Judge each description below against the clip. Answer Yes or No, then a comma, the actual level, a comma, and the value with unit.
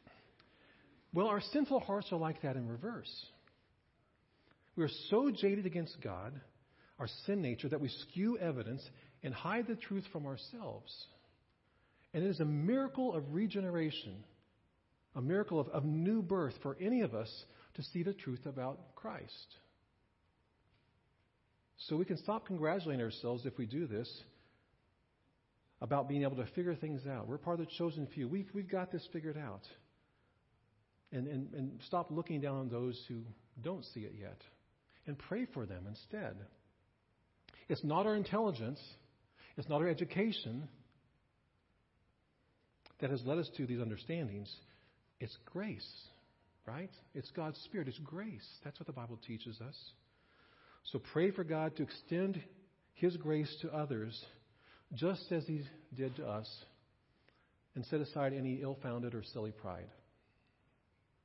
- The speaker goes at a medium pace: Yes, average, 150 wpm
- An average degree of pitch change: No, wide, 6.6 semitones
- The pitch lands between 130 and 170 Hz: Yes, low, 135 Hz